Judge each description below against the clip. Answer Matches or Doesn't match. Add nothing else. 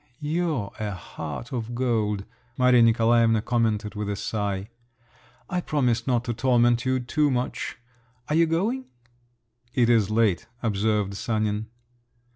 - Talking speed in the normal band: Doesn't match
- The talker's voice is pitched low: Matches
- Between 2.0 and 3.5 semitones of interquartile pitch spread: Matches